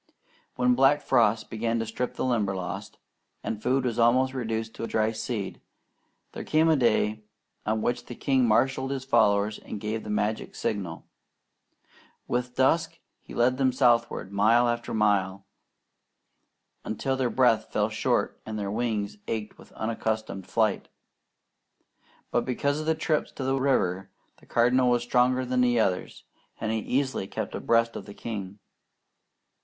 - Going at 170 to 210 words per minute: No, average, 155 wpm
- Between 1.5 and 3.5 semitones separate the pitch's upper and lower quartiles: Yes, average, 3.0 semitones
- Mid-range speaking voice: No, low, 115 Hz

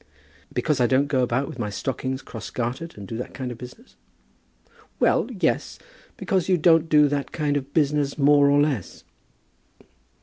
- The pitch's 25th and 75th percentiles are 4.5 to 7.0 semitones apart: No, average, 3.2 semitones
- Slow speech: No, average, 170 wpm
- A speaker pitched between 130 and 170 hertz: Yes, medium, 140 Hz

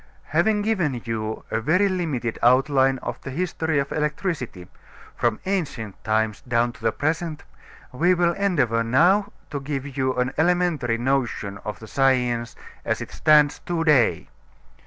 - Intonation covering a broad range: Yes, wide, 5.9 semitones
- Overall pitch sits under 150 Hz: Yes, low, 135 Hz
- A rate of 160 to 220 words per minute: No, average, 150 wpm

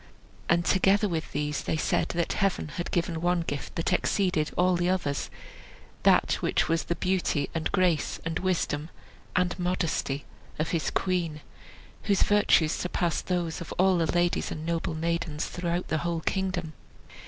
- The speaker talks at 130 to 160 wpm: Yes, average, 155 wpm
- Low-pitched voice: No, medium, 170 Hz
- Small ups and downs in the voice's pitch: Yes, narrow, 2.2 semitones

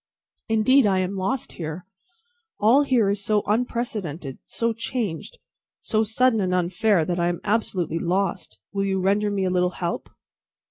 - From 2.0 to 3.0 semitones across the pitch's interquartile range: No, average, 3.7 semitones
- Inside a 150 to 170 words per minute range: Yes, average, 155 wpm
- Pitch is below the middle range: No, high, 200 Hz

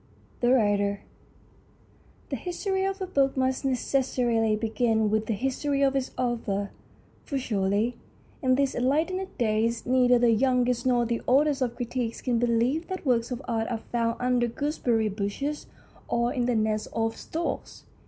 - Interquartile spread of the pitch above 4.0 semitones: No, average, 3.0 semitones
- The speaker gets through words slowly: No, average, 155 wpm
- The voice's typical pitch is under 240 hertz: No, high, 245 Hz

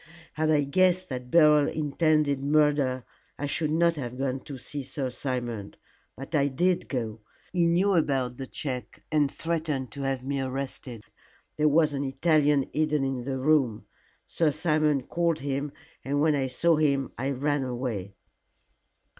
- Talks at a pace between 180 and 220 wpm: No, average, 160 wpm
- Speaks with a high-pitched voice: No, medium, 140 Hz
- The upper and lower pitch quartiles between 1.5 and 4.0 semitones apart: Yes, average, 2.7 semitones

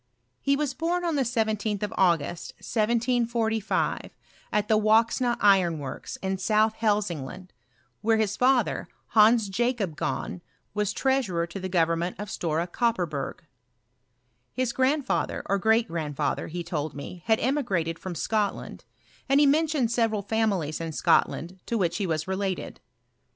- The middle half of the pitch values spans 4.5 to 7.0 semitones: Yes, average, 5.2 semitones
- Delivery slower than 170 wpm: Yes, average, 145 wpm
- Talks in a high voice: Yes, high, 210 Hz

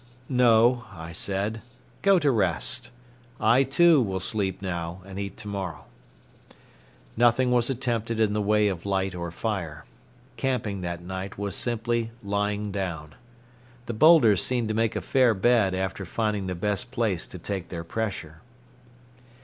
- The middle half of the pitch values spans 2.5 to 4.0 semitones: Yes, average, 3.7 semitones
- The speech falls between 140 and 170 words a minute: Yes, average, 150 wpm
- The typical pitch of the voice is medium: No, low, 105 Hz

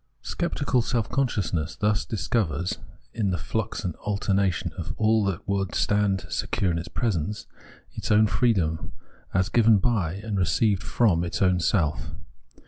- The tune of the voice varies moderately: Yes, average, 3.8 semitones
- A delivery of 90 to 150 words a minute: Yes, average, 145 wpm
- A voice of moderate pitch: No, low, 100 Hz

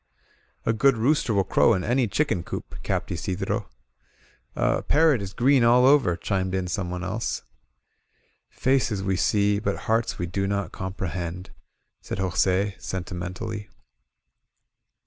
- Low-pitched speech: Yes, low, 100 Hz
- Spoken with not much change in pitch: No, average, 3.9 semitones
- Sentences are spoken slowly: Yes, slow, 130 wpm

